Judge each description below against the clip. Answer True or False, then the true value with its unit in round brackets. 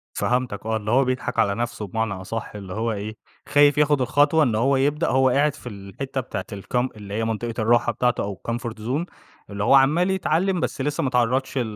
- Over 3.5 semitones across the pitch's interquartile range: True (4.2 semitones)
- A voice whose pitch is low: True (120 Hz)